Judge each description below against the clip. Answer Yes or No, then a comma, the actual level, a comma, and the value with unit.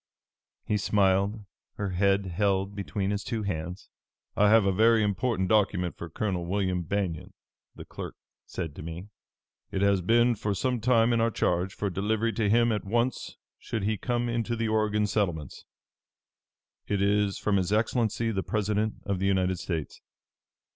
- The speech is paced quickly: No, average, 165 wpm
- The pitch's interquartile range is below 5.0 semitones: Yes, average, 2.7 semitones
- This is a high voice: No, low, 100 Hz